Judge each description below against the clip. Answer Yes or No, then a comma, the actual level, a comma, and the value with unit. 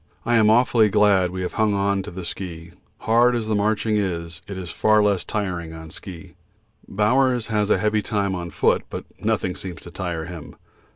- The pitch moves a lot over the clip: No, average, 3.4 semitones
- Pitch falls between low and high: No, low, 100 Hz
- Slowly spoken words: No, average, 195 wpm